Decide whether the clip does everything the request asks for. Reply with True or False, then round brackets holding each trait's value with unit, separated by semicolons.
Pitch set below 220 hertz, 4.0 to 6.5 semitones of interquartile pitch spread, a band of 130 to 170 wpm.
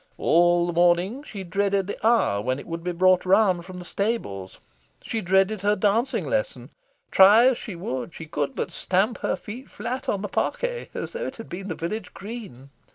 False (190 Hz; 4.4 semitones; 200 wpm)